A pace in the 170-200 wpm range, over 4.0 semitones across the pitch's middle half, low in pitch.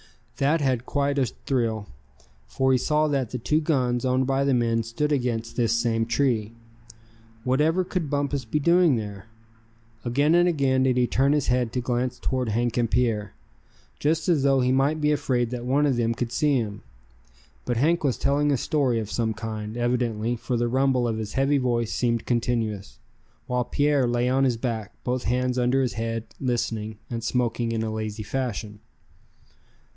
No: average, 185 wpm; average, 3.1 semitones; low, 125 Hz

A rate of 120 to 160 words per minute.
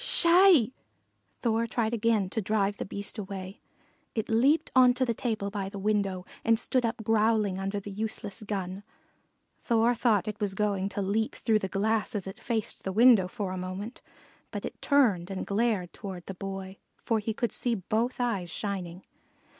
No: average, 180 wpm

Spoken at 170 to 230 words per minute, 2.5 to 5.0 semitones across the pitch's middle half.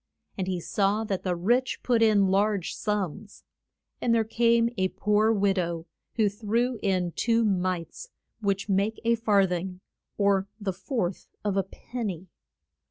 No: average, 160 wpm; average, 3.1 semitones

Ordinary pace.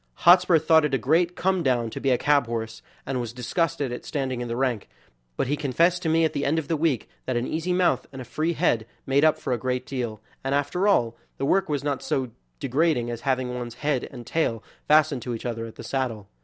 No: fast, 245 wpm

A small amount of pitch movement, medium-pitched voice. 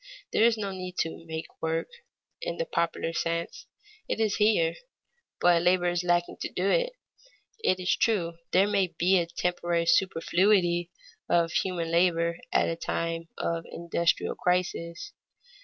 Yes: narrow, 2.0 semitones; medium, 175 Hz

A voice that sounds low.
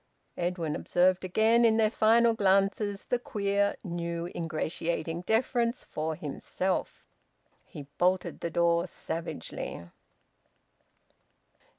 No: medium, 185 Hz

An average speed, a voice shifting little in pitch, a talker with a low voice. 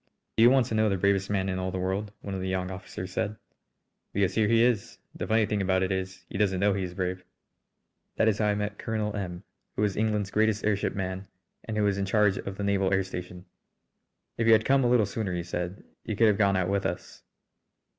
No: fast, 245 wpm; narrow, 2.3 semitones; low, 100 Hz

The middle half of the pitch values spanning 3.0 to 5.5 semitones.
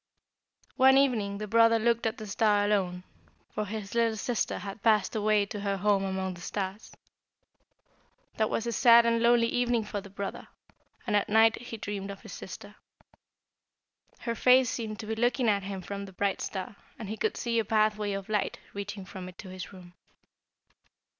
No: narrow, 2.6 semitones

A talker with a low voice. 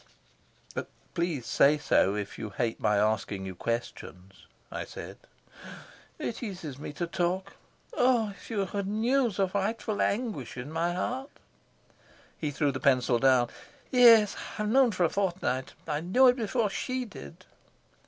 No: medium, 180 Hz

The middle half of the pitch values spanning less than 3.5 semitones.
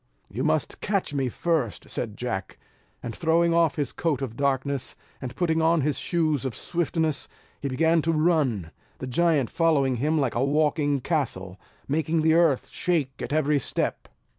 No: average, 3.8 semitones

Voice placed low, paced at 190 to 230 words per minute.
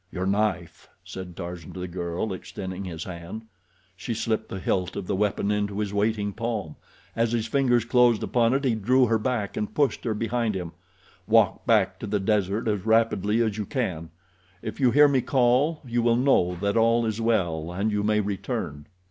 Yes: low, 105 Hz; average, 195 wpm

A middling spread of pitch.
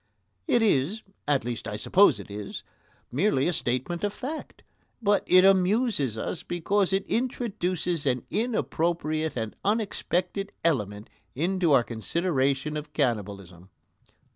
No: wide, 7.6 semitones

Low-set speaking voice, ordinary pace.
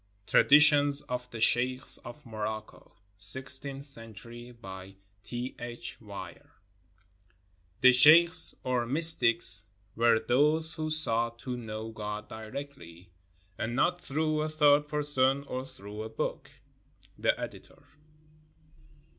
No: low, 125 Hz; slow, 115 wpm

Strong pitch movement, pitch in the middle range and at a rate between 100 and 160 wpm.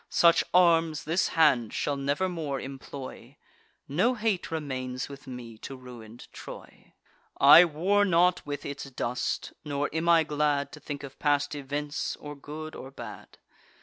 No: average, 3.2 semitones; medium, 145 Hz; average, 150 wpm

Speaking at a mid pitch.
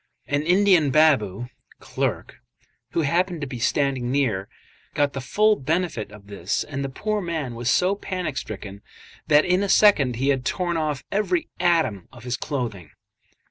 Yes: medium, 145 Hz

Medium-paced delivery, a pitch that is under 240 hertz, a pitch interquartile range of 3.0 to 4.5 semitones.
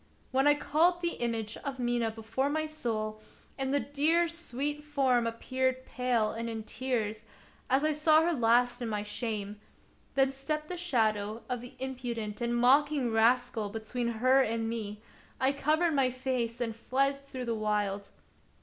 No: average, 170 wpm; very high, 250 Hz; average, 3.8 semitones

